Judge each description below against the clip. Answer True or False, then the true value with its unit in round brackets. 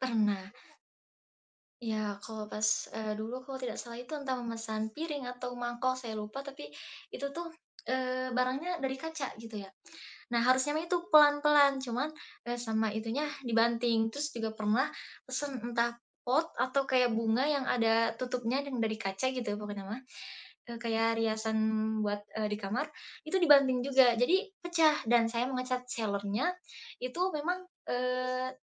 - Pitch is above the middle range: True (245 Hz)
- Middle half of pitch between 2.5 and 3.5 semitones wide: True (3.2 semitones)